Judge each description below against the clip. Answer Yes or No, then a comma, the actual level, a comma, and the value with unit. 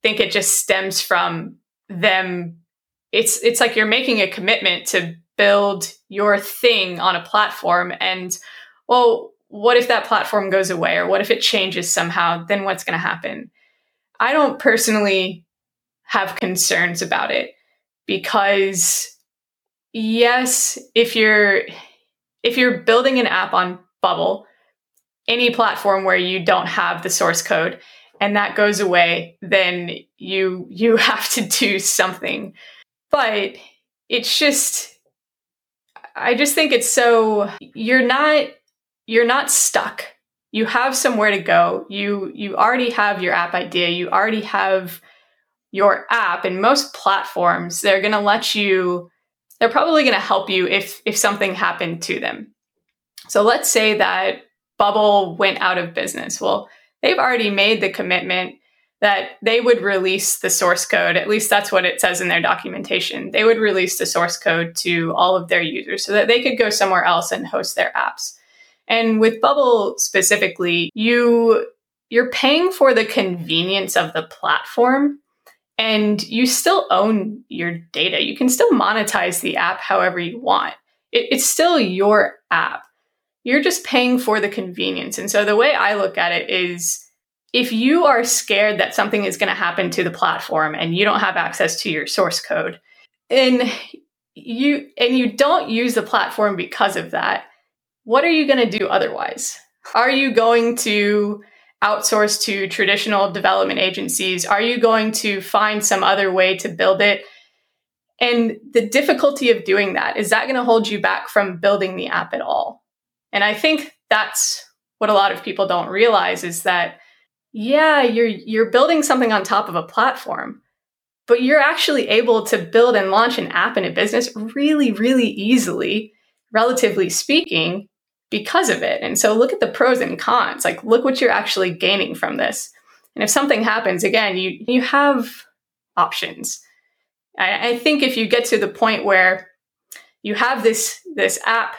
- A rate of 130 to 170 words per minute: Yes, average, 165 wpm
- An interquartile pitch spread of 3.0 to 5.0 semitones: Yes, average, 4.2 semitones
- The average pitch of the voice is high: Yes, high, 215 Hz